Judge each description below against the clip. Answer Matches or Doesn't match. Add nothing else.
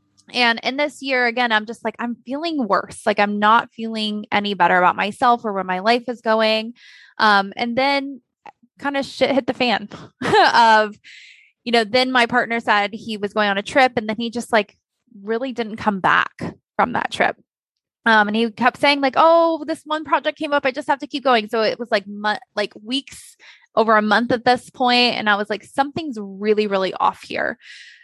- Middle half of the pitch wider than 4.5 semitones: Doesn't match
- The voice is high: Matches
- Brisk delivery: Matches